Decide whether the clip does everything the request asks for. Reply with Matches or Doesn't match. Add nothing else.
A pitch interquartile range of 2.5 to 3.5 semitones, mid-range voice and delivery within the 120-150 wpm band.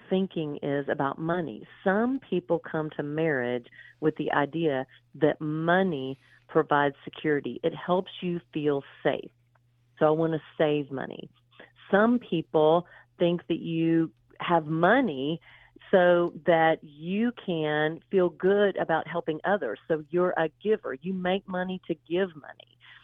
Matches